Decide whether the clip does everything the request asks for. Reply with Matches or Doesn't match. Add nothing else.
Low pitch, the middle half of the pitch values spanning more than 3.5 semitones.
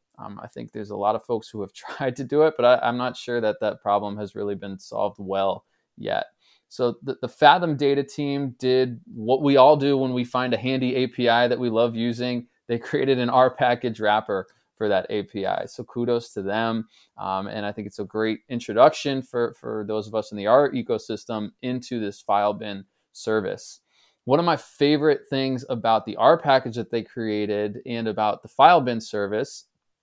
Doesn't match